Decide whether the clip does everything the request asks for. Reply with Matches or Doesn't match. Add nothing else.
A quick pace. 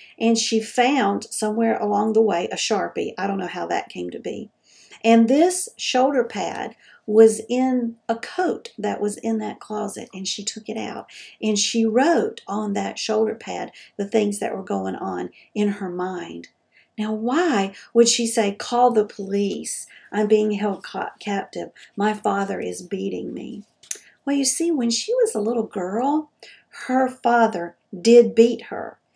Doesn't match